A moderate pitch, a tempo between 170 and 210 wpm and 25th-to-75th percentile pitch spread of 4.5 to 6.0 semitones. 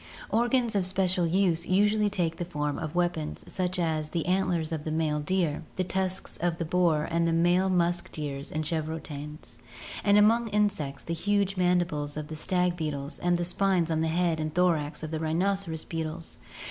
No: medium, 170 Hz; average, 185 wpm; average, 3.0 semitones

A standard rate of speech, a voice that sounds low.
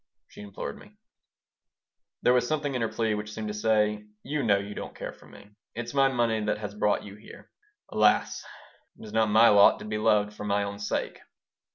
No: fast, 210 wpm; low, 105 Hz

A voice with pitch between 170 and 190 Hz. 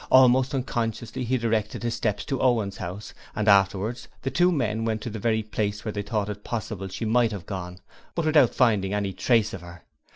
No: low, 110 Hz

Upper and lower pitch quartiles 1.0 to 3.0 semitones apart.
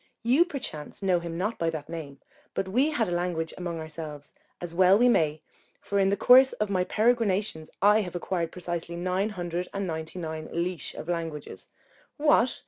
No: average, 4.0 semitones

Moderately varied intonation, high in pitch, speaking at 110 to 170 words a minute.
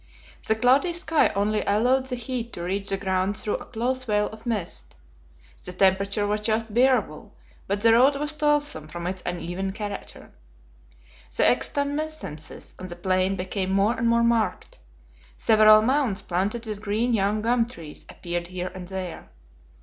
Yes: average, 4.1 semitones; high, 210 Hz; average, 160 wpm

